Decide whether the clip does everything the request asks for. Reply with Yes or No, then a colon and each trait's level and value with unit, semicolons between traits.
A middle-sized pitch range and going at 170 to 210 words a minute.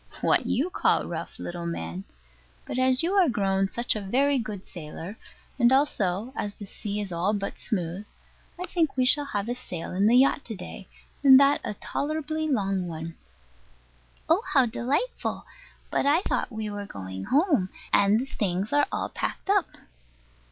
No: wide, 6.4 semitones; average, 175 wpm